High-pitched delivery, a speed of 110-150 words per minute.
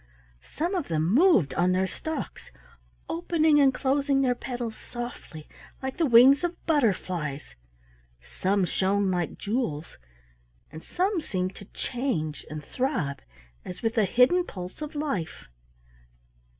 Yes: high, 235 Hz; slow, 135 wpm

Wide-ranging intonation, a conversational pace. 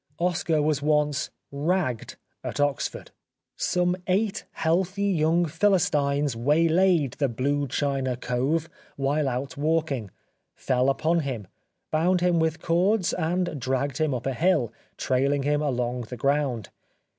No: average, 3.8 semitones; average, 145 wpm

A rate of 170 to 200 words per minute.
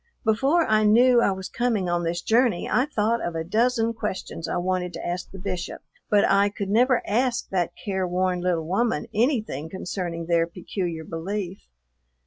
Yes: average, 175 wpm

